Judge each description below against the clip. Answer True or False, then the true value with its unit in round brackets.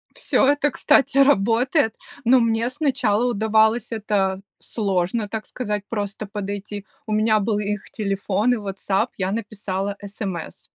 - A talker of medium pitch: False (215 Hz)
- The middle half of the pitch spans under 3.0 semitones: True (2.5 semitones)